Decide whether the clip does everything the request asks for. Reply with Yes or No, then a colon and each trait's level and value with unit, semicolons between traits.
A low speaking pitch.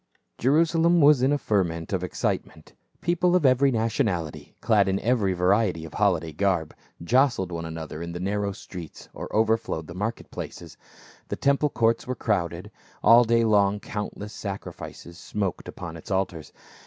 Yes: low, 100 Hz